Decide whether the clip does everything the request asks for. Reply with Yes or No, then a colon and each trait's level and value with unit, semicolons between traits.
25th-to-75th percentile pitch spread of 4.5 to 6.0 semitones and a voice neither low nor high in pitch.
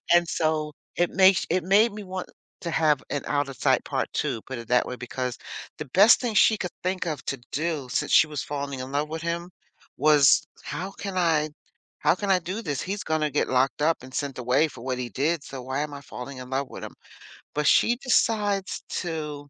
Yes: average, 5.0 semitones; medium, 155 Hz